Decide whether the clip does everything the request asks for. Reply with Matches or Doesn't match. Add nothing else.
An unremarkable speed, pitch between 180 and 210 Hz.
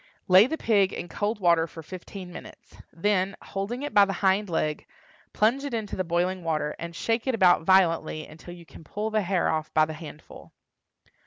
Matches